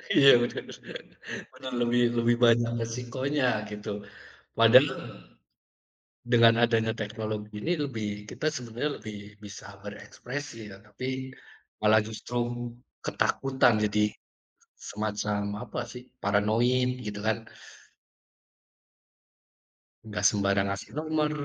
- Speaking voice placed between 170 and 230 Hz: No, low, 110 Hz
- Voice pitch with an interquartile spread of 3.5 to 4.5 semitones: No, average, 2.9 semitones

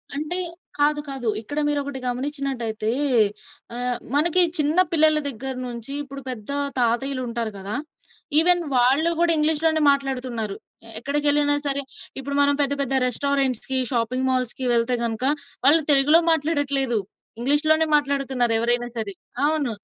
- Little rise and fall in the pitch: No, average, 3.3 semitones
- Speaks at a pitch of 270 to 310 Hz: Yes, very high, 275 Hz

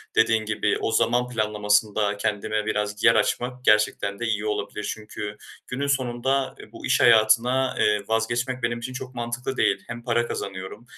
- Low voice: Yes, low, 115 Hz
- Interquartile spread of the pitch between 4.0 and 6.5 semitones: No, narrow, 2.6 semitones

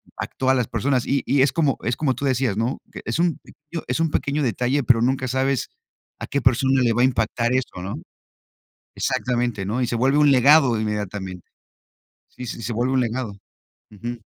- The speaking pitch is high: No, low, 125 Hz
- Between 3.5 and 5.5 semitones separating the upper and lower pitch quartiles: No, average, 2.7 semitones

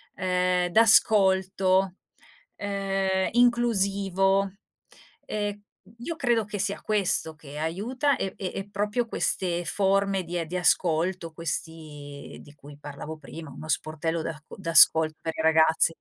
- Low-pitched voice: No, medium, 185 Hz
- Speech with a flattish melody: No, average, 3.7 semitones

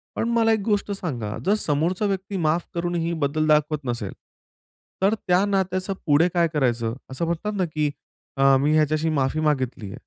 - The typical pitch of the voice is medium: Yes, medium, 155 Hz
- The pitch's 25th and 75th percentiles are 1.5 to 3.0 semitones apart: No, average, 4.8 semitones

